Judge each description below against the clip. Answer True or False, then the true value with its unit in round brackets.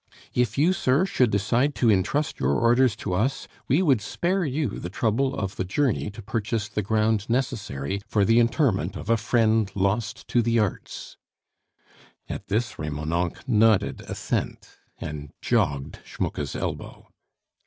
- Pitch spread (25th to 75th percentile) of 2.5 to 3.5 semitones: False (4.2 semitones)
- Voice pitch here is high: False (110 Hz)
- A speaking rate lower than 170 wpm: True (155 wpm)